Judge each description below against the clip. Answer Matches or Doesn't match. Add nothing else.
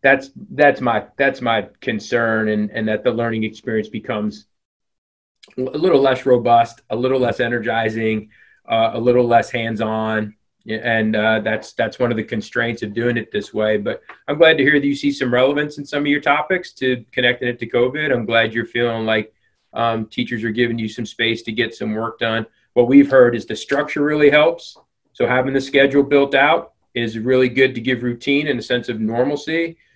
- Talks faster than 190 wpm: Matches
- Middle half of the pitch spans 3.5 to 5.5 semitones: Doesn't match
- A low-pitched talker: Matches